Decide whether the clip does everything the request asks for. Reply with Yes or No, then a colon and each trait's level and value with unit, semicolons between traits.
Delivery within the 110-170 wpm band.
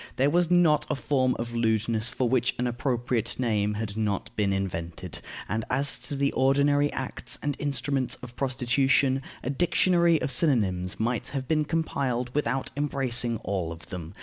Yes: average, 165 wpm